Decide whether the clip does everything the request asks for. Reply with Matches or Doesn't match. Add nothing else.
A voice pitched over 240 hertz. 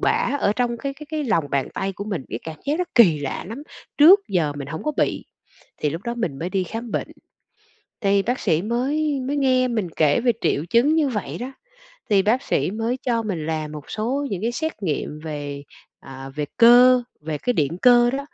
Doesn't match